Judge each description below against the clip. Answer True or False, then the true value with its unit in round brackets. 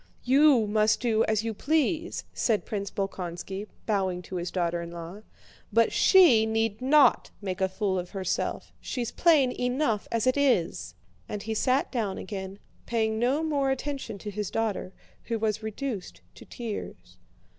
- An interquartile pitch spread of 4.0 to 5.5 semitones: True (4.6 semitones)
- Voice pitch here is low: False (220 Hz)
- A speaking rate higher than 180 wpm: False (160 wpm)